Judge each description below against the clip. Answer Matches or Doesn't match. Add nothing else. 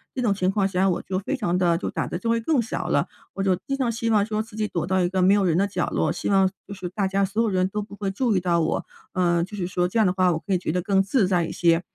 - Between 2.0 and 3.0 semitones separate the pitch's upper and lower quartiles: Matches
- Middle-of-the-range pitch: Doesn't match